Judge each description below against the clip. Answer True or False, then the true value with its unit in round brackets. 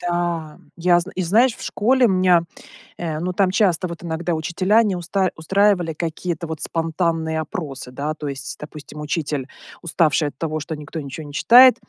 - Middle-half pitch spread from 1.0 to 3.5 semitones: True (2.9 semitones)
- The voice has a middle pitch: True (170 Hz)